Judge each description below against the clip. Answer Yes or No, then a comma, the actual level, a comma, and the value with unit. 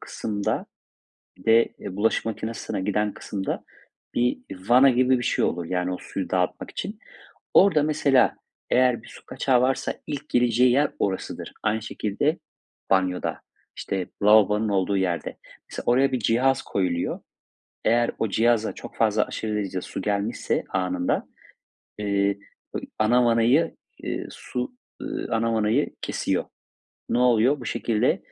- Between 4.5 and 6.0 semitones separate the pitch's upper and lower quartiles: No, average, 3.8 semitones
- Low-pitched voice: Yes, low, 110 Hz